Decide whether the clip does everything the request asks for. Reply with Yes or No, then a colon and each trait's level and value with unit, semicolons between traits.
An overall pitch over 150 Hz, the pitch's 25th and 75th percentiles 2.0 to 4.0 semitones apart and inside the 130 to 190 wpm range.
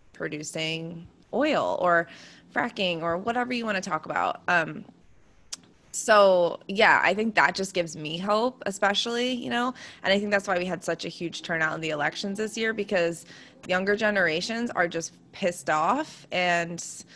No: medium, 185 Hz; average, 4.5 semitones; average, 170 wpm